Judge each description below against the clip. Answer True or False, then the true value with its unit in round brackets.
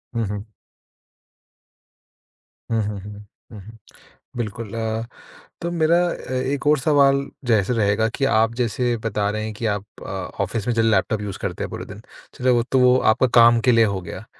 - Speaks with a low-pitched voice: True (115 Hz)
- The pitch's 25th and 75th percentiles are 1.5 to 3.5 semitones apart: True (3.1 semitones)